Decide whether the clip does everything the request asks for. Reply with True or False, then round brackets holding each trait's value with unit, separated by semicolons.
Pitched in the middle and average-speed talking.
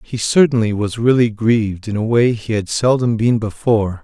False (110 Hz; 195 wpm)